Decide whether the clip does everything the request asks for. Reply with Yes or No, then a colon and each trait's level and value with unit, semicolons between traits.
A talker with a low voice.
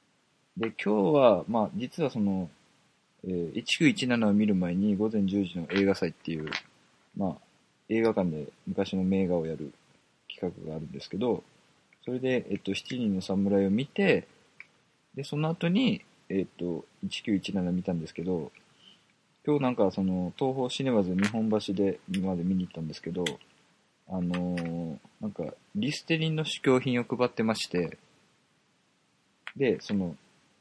Yes: low, 100 Hz